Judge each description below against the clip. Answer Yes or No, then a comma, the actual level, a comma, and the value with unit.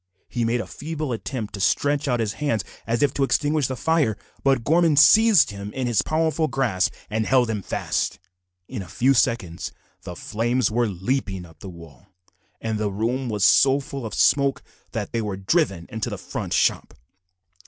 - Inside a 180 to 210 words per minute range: Yes, average, 185 wpm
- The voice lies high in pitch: No, low, 120 Hz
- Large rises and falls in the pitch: No, average, 5.0 semitones